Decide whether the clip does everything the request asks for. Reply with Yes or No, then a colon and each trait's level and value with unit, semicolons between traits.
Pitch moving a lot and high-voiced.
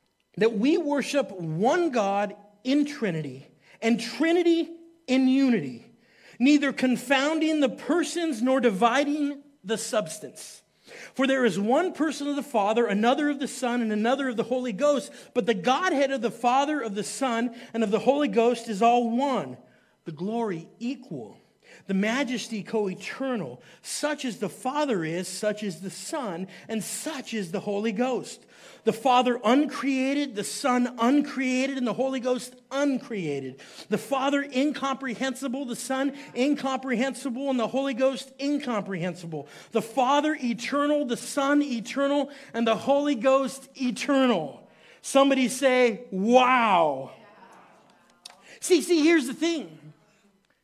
No: average, 4.0 semitones; very high, 255 Hz